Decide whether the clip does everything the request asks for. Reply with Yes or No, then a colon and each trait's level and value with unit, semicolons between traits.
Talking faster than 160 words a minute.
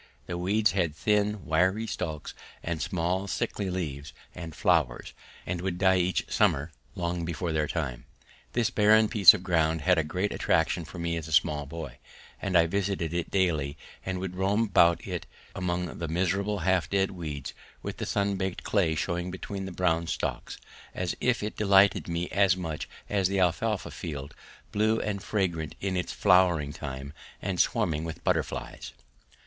Yes: average, 170 wpm